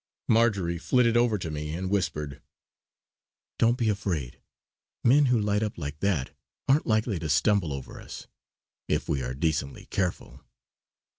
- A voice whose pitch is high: No, very low, 95 Hz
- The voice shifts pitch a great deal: Yes, wide, 6.6 semitones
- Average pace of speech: Yes, average, 145 wpm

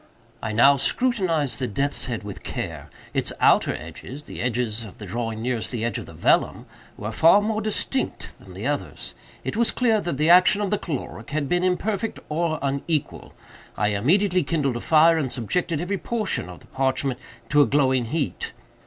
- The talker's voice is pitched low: No, medium, 145 Hz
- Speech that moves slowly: No, average, 180 wpm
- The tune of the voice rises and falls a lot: Yes, wide, 6.9 semitones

